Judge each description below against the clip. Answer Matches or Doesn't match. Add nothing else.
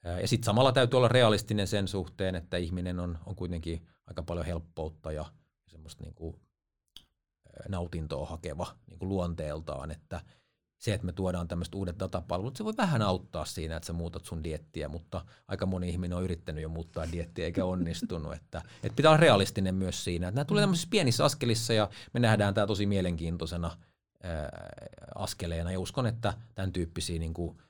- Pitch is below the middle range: Matches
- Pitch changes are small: Doesn't match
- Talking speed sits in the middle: Doesn't match